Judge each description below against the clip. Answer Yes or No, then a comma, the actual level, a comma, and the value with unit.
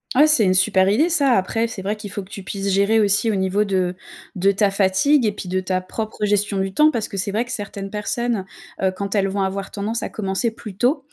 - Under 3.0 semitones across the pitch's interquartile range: Yes, narrow, 2.6 semitones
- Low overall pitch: No, high, 200 Hz